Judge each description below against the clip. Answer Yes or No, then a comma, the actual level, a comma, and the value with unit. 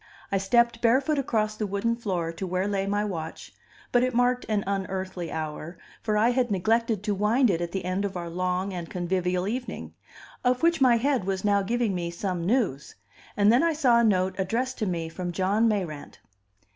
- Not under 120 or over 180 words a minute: No, average, 200 wpm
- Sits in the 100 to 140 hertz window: No, high, 200 Hz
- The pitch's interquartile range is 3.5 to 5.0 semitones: Yes, average, 4.4 semitones